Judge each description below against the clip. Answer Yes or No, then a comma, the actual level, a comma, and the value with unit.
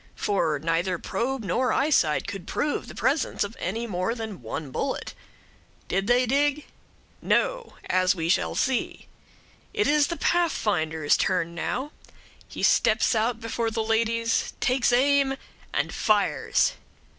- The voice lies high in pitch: Yes, high, 225 Hz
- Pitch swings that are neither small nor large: No, wide, 6.4 semitones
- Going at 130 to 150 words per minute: Yes, slow, 135 wpm